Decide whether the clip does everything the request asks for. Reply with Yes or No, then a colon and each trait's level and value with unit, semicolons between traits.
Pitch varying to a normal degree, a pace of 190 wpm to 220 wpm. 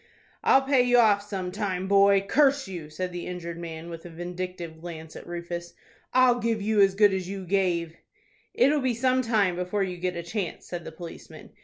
Yes: average, 3.8 semitones; average, 200 wpm